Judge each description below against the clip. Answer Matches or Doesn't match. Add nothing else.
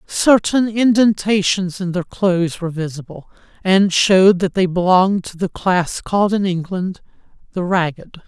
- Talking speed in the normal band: Matches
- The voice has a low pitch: Doesn't match